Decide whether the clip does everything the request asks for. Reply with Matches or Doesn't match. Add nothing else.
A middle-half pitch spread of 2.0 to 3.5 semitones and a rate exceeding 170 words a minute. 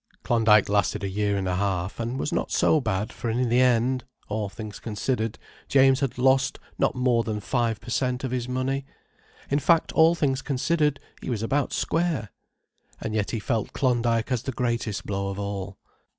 Doesn't match